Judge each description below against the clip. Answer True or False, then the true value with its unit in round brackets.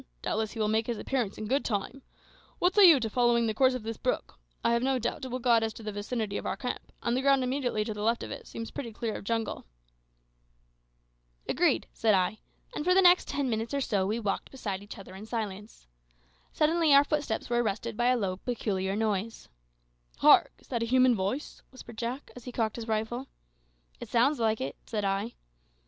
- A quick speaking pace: True (220 wpm)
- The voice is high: True (230 Hz)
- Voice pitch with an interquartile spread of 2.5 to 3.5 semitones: True (3.2 semitones)